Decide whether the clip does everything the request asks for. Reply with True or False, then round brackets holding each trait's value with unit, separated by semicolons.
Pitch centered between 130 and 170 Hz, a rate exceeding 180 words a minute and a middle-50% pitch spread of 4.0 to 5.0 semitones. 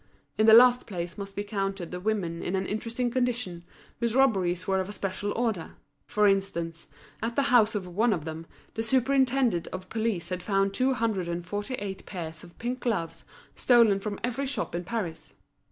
False (205 Hz; 190 wpm; 4.6 semitones)